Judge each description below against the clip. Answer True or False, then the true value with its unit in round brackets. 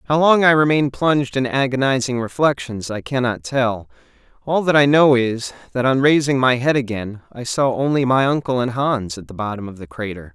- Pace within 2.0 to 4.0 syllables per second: False (5.4 syllables/s)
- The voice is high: False (125 Hz)